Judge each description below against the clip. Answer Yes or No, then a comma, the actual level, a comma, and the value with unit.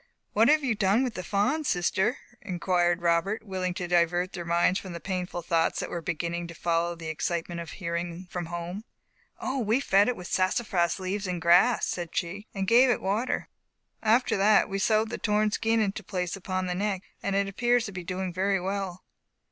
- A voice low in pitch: No, medium, 185 Hz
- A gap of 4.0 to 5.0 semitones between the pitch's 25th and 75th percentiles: No, average, 3.2 semitones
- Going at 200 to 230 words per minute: Yes, fast, 205 wpm